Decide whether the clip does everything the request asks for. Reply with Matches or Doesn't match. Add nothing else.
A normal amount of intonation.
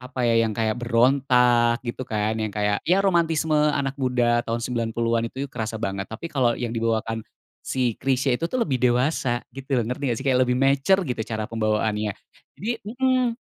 Matches